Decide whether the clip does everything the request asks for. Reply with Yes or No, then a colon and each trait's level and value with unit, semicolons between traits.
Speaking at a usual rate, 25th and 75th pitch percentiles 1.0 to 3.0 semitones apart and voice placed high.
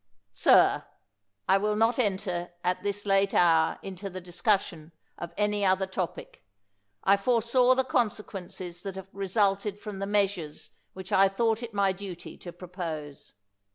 Yes: average, 155 wpm; narrow, 2.5 semitones; high, 195 Hz